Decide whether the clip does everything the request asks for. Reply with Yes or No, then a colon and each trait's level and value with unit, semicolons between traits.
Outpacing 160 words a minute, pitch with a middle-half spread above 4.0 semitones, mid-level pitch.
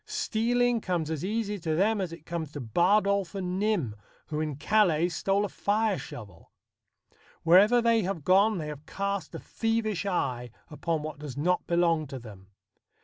Yes: average, 170 wpm; average, 5.3 semitones; medium, 180 Hz